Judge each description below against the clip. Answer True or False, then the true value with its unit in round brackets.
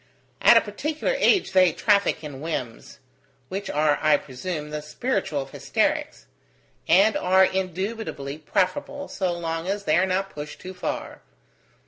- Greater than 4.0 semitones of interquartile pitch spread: True (4.8 semitones)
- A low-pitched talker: False (185 Hz)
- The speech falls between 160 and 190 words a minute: False (145 wpm)